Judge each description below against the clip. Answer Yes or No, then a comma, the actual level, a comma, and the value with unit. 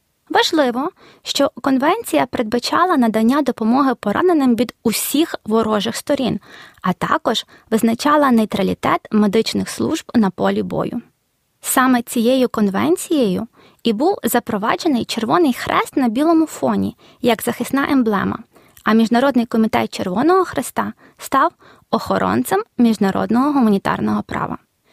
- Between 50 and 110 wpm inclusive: Yes, slow, 105 wpm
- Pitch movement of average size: Yes, average, 4.6 semitones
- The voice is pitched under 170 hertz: No, high, 245 Hz